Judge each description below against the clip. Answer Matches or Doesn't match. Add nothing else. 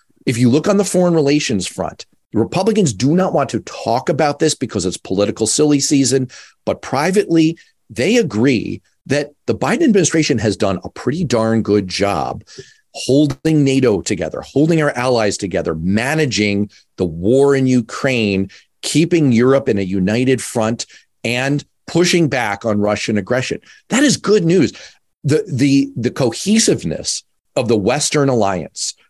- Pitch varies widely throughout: Matches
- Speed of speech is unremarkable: Matches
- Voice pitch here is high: Doesn't match